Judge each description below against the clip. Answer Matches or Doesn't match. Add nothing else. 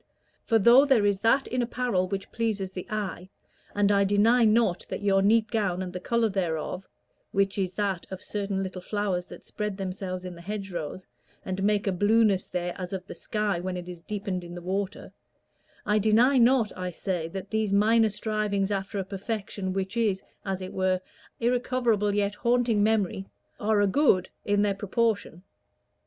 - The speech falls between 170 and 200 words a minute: Matches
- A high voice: Matches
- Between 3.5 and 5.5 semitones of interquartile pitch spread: Doesn't match